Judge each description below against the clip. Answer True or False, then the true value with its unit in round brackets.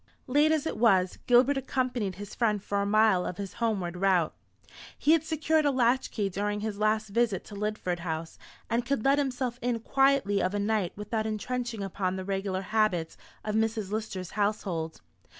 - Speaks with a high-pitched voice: True (215 Hz)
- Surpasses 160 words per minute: True (185 wpm)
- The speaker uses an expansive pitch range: False (3.8 semitones)